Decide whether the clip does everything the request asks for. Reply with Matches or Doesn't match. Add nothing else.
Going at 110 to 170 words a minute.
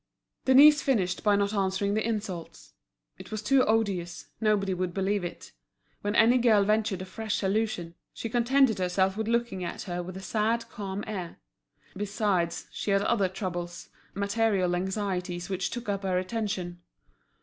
Matches